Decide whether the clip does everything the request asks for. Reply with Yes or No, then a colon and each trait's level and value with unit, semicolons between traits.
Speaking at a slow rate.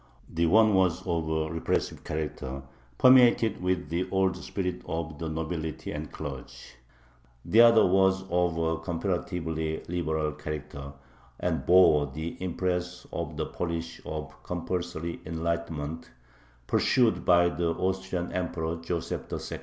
Yes: slow, 130 wpm